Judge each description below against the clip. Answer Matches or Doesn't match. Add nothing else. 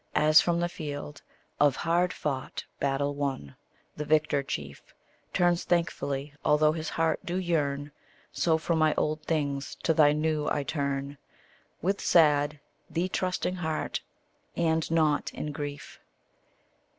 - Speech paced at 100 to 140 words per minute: Matches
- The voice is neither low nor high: Matches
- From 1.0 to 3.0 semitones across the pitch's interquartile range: Matches